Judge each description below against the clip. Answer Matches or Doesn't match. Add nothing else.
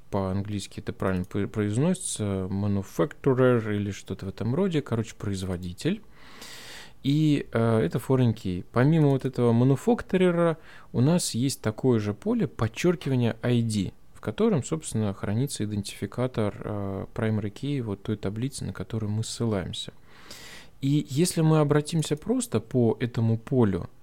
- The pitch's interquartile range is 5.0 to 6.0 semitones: Matches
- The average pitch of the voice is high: Doesn't match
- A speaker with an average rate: Matches